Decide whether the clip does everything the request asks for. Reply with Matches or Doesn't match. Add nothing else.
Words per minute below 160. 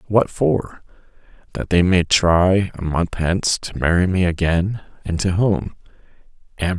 Matches